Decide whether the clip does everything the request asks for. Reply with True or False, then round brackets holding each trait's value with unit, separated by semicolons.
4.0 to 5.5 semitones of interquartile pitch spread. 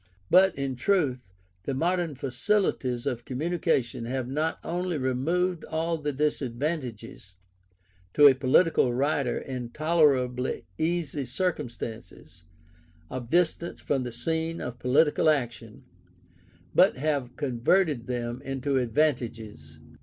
True (4.6 semitones)